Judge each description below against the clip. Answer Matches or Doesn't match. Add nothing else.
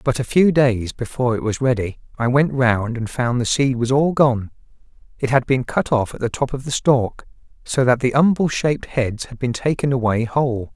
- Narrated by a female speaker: Doesn't match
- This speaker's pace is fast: Matches